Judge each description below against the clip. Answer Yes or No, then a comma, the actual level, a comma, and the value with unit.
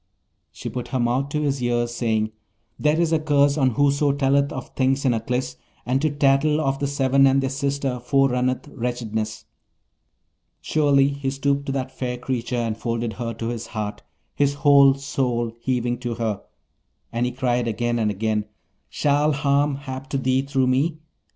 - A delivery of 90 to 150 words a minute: No, average, 175 wpm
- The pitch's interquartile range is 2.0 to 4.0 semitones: Yes, average, 2.8 semitones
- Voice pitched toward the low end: Yes, low, 130 Hz